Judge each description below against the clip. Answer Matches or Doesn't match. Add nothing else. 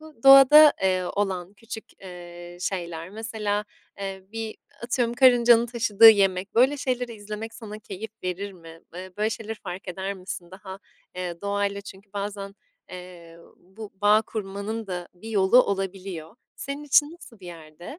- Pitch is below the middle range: Doesn't match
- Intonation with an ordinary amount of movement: Matches